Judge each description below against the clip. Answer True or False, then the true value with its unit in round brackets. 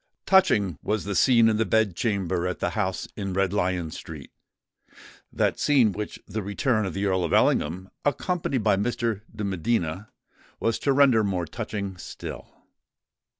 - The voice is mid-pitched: False (100 Hz)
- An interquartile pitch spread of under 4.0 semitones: True (3.4 semitones)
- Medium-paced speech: True (155 wpm)